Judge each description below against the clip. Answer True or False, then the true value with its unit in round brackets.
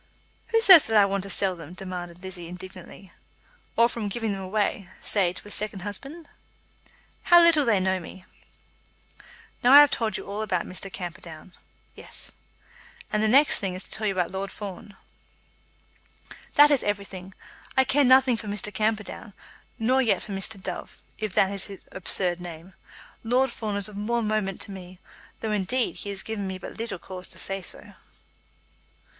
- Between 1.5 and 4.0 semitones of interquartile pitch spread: True (3.1 semitones)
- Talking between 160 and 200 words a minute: True (180 wpm)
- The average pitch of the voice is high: True (200 Hz)